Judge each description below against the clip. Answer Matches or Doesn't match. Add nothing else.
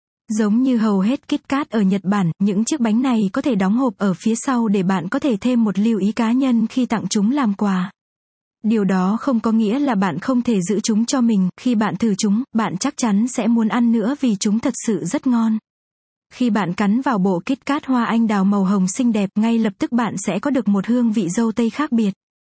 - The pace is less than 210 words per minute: Doesn't match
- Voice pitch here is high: Matches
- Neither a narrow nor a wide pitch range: Matches